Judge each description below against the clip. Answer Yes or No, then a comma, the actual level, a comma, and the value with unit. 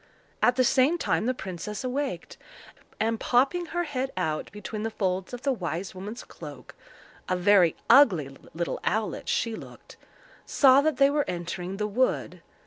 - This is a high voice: Yes, high, 220 Hz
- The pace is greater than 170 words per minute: No, average, 150 wpm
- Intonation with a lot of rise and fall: Yes, wide, 6.3 semitones